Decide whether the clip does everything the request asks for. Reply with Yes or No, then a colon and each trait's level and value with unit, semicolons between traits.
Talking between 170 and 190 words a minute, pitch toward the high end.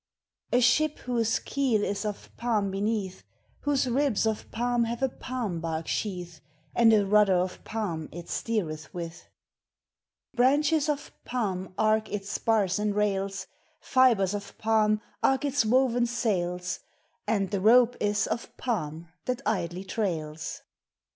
No: average, 140 wpm; high, 210 Hz